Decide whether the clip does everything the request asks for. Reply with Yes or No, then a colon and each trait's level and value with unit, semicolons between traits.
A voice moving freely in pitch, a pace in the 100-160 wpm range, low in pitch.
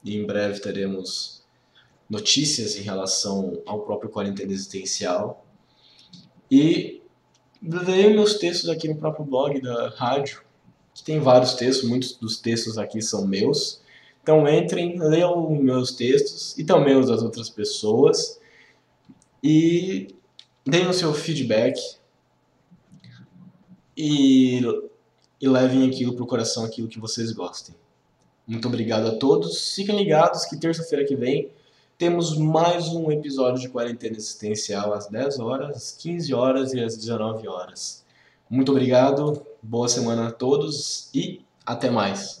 Yes: wide, 6.5 semitones; average, 135 wpm; low, 130 Hz